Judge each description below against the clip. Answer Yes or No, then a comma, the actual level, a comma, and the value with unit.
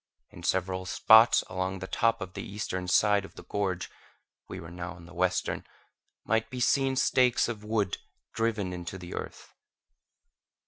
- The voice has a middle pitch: No, very low, 95 Hz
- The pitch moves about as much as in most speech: Yes, average, 3.5 semitones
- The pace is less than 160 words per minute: No, average, 165 wpm